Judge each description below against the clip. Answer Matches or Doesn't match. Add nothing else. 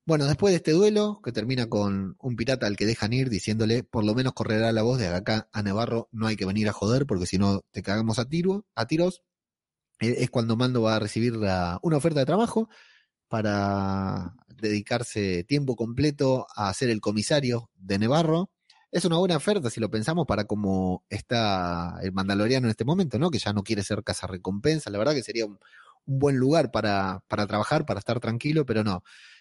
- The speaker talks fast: Matches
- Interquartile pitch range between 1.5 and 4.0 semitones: Doesn't match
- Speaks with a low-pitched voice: Matches